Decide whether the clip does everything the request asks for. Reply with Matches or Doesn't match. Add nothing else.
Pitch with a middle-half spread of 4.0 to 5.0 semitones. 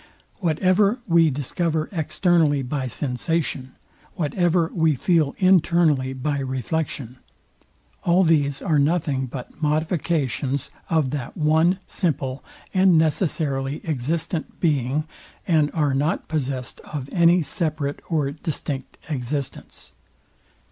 Doesn't match